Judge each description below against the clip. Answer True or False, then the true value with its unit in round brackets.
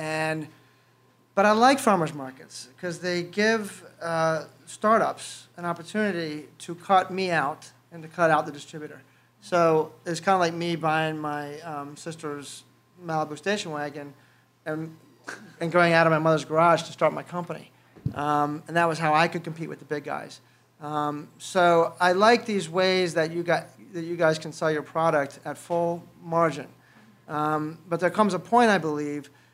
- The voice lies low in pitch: False (160 Hz)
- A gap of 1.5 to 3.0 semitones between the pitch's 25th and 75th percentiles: True (2.6 semitones)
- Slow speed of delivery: False (175 wpm)